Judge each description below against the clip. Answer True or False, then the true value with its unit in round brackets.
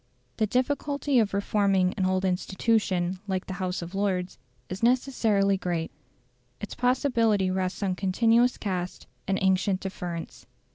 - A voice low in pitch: False (195 Hz)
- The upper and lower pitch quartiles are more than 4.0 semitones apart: False (3.5 semitones)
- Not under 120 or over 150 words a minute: True (135 wpm)